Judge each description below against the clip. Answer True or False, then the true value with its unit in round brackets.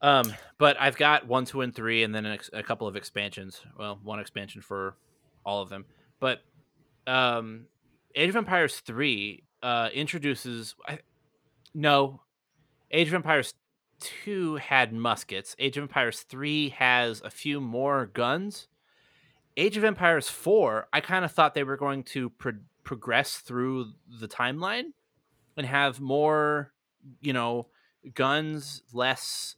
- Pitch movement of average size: True (4.0 semitones)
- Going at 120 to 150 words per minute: True (145 wpm)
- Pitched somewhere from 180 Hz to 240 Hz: False (135 Hz)